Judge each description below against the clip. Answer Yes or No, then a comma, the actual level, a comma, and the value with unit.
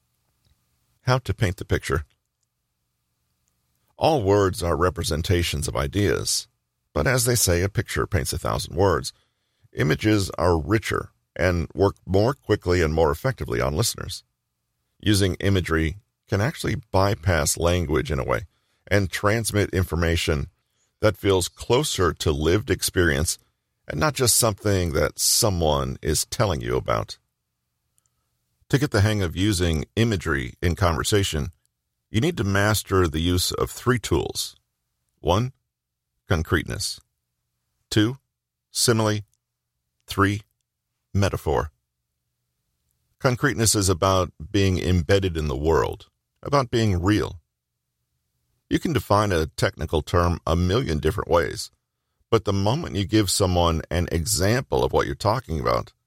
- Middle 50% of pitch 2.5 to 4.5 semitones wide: No, wide, 5.5 semitones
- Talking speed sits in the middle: No, slow, 125 wpm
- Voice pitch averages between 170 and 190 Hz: No, very low, 90 Hz